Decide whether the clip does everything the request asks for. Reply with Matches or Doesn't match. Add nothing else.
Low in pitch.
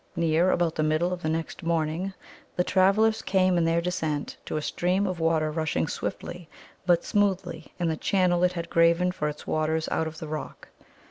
Doesn't match